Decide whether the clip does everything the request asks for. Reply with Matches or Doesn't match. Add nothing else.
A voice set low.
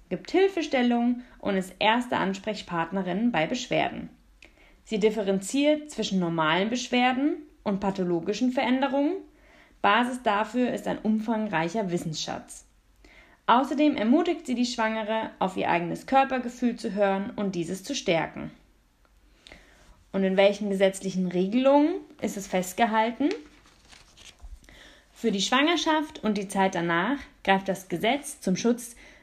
Doesn't match